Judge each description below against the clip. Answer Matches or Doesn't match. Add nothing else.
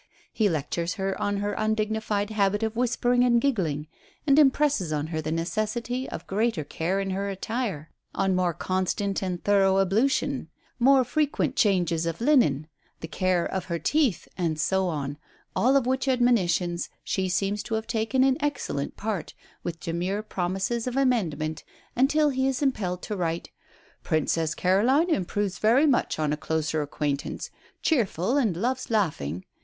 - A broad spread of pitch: Matches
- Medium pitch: Doesn't match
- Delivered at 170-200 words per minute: Doesn't match